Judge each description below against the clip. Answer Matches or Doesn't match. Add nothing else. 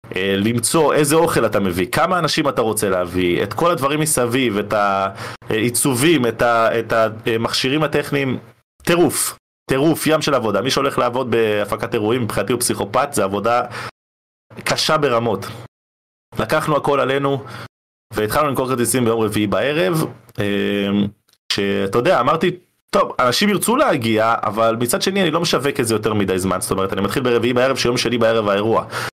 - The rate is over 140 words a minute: Matches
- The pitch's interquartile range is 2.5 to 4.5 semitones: Doesn't match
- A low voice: Matches